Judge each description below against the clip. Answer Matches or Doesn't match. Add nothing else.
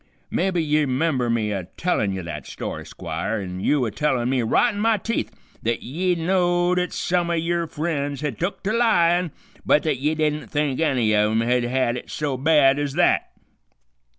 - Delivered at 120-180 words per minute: Doesn't match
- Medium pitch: Matches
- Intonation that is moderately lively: Doesn't match